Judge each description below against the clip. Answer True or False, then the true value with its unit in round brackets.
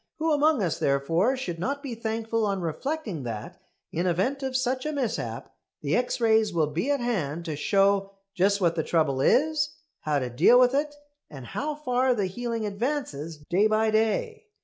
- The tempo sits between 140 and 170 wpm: False (185 wpm)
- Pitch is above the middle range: True (215 Hz)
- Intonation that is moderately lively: False (7.4 semitones)